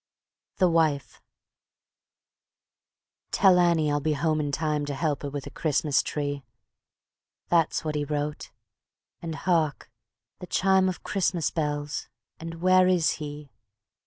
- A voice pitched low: No, medium, 155 Hz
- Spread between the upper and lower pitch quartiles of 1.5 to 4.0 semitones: Yes, average, 2.8 semitones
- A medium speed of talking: No, slow, 130 wpm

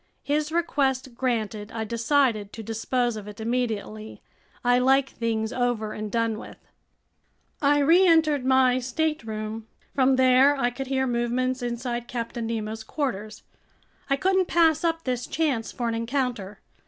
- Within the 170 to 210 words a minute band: No, average, 140 wpm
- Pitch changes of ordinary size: Yes, average, 3.4 semitones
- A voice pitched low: No, high, 245 Hz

